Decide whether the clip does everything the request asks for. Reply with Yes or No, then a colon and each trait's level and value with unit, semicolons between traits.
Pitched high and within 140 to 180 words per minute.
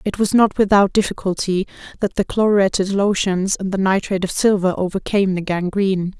Yes: high, 195 Hz; average, 165 wpm